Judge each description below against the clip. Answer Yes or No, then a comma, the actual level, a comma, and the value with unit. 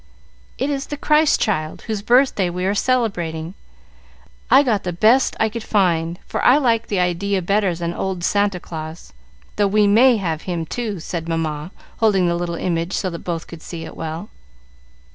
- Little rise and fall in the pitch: No, average, 4.6 semitones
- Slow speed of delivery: No, average, 180 wpm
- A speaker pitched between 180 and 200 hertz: Yes, medium, 185 Hz